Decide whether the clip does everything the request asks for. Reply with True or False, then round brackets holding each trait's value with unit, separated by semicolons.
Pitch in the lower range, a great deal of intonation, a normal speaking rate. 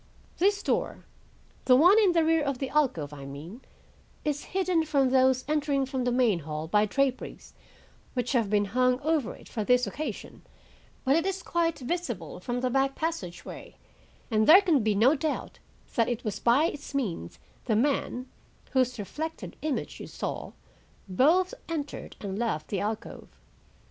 False (260 Hz; 6.1 semitones; 165 wpm)